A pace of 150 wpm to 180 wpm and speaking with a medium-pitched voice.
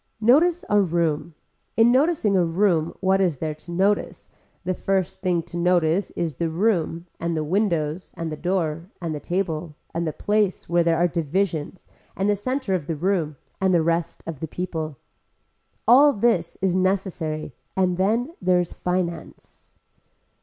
Yes: average, 165 wpm; medium, 175 Hz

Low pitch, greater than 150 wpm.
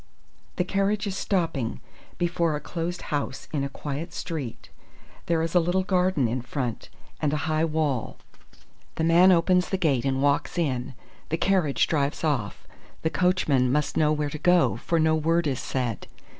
No: medium, 155 Hz; average, 170 wpm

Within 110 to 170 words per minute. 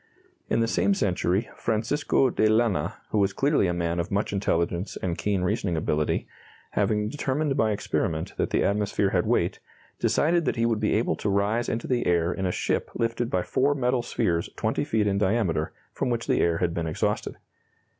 No: average, 195 wpm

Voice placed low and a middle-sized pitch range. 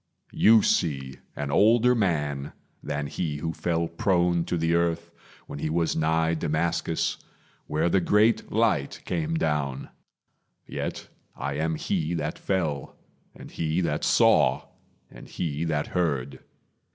Yes: very low, 80 Hz; average, 3.0 semitones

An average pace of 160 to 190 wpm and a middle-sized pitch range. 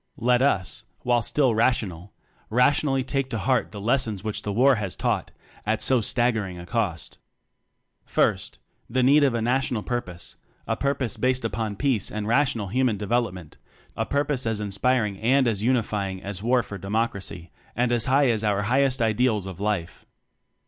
Yes: average, 170 wpm; average, 3.9 semitones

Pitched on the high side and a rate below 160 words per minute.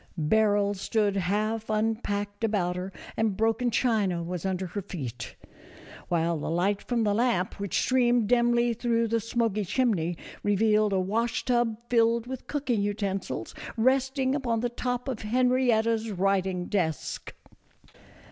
Yes: high, 215 Hz; average, 140 wpm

